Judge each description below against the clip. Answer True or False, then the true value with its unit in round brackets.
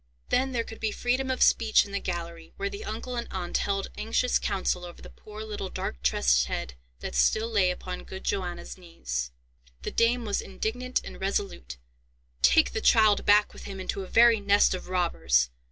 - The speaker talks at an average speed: True (190 wpm)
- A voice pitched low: False (200 Hz)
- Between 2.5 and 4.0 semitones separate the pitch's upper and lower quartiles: False (4.5 semitones)